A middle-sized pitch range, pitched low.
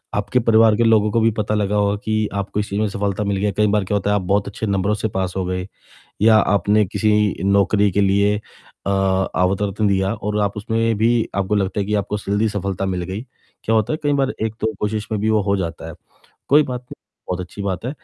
No: narrow, 1.6 semitones; low, 105 Hz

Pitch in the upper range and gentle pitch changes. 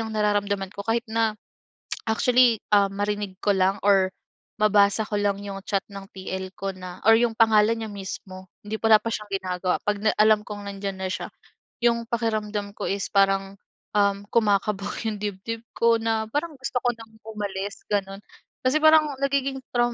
Yes: high, 210 Hz; narrow, 2.3 semitones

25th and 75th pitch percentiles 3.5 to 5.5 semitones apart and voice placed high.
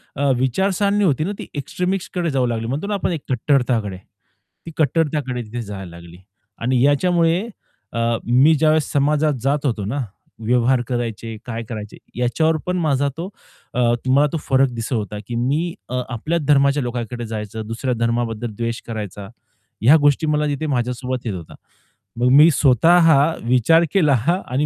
No: average, 4.8 semitones; low, 130 Hz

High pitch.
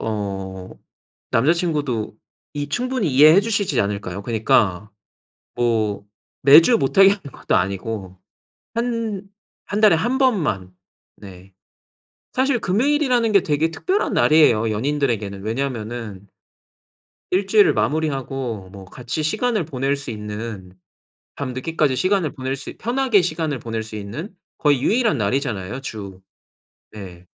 No: low, 135 Hz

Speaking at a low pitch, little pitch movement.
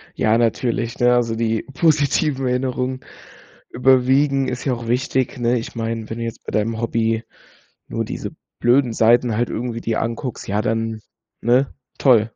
Yes: low, 120 Hz; narrow, 2.2 semitones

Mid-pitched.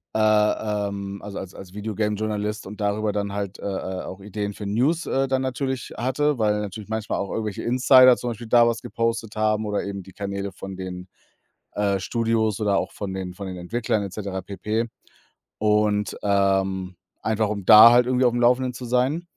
No: low, 105 Hz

